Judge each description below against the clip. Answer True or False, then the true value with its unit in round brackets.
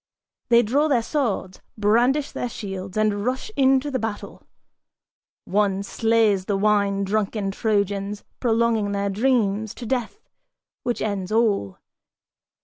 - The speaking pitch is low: False (215 Hz)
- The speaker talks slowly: True (125 wpm)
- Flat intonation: False (3.0 semitones)